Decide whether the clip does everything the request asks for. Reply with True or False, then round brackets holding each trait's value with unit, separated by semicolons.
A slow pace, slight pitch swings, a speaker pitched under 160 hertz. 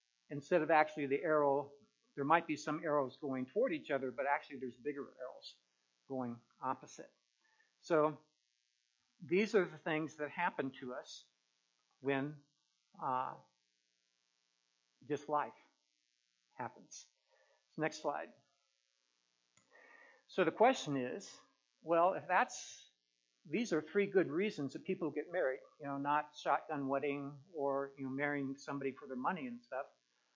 False (130 wpm; 4.7 semitones; 140 Hz)